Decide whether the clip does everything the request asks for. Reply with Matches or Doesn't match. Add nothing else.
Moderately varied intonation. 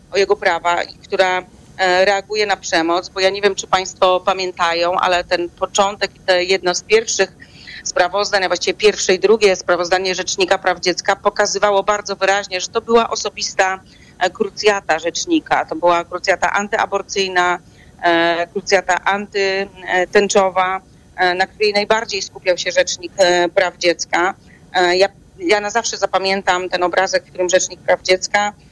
Doesn't match